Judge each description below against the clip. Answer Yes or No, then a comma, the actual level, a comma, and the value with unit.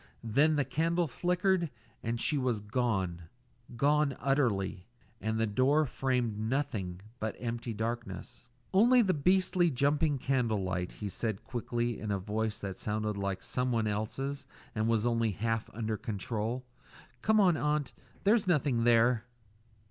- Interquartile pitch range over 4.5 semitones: Yes, average, 5.0 semitones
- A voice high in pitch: No, low, 120 Hz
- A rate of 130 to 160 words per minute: Yes, average, 140 wpm